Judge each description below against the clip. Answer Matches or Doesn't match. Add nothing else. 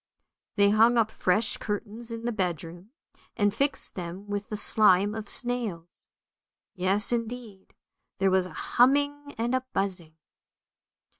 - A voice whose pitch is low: Doesn't match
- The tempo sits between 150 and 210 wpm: Doesn't match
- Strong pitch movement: Doesn't match